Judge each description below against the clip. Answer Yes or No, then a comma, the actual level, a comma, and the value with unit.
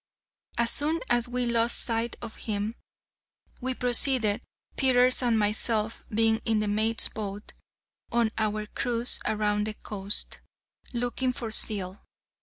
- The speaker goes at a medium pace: No, slow, 130 wpm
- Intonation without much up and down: Yes, narrow, 2.3 semitones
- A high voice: Yes, high, 225 Hz